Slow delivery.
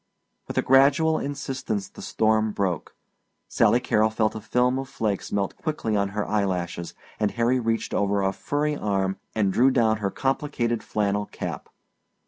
No: average, 160 wpm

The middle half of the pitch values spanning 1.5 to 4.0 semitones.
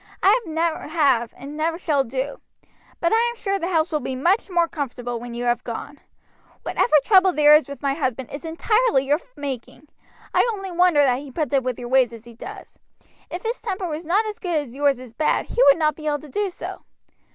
No: average, 5.0 semitones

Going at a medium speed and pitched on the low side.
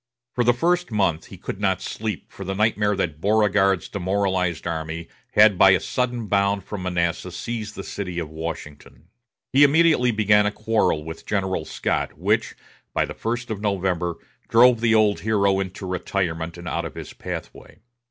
Yes: average, 170 wpm; low, 100 Hz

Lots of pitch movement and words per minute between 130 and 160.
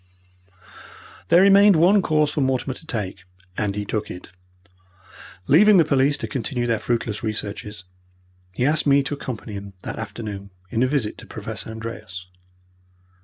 Yes: wide, 6.0 semitones; average, 155 wpm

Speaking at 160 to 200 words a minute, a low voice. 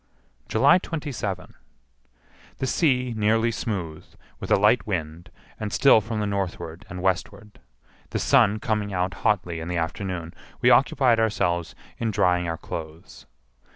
No: average, 140 wpm; low, 100 Hz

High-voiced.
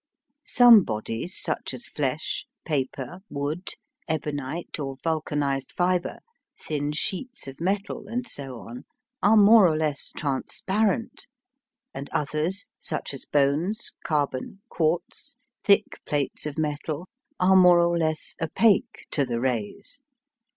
No: medium, 155 Hz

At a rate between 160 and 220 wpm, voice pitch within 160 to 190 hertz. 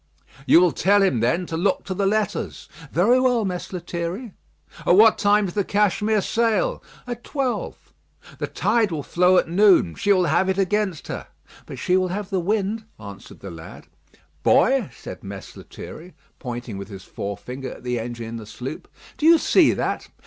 Yes: average, 185 wpm; medium, 185 Hz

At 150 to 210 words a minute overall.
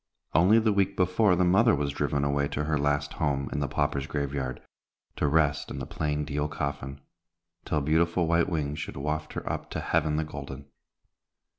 Yes: average, 190 wpm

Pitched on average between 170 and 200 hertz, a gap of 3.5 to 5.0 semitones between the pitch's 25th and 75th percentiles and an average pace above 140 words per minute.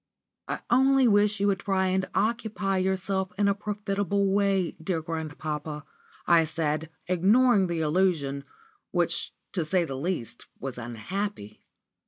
No: high, 190 Hz; average, 4.1 semitones; slow, 135 wpm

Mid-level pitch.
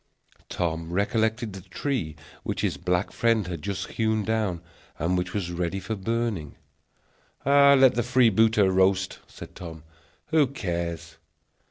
No: low, 100 Hz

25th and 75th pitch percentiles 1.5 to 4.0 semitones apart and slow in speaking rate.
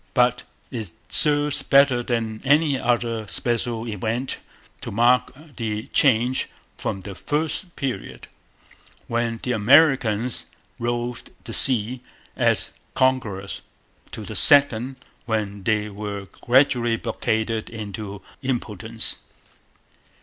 Yes: average, 3.0 semitones; slow, 105 wpm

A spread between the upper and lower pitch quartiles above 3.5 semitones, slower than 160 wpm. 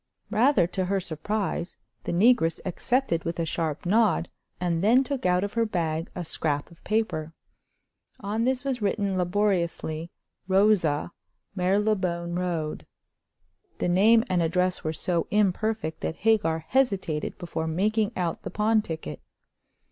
Yes: average, 4.4 semitones; average, 140 wpm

